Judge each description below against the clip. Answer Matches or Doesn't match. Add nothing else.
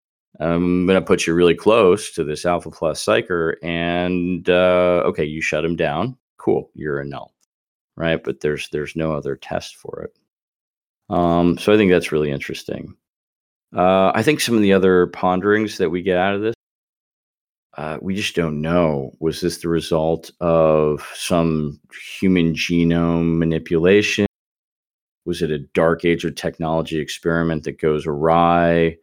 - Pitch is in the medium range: Doesn't match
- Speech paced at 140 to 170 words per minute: Matches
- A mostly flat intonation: Matches